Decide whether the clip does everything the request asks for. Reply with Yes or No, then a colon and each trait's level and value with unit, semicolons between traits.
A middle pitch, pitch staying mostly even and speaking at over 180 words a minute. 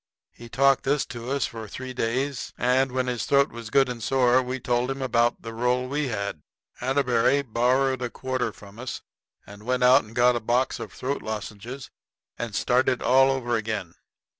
No: low, 125 Hz; narrow, 2.2 semitones; average, 190 wpm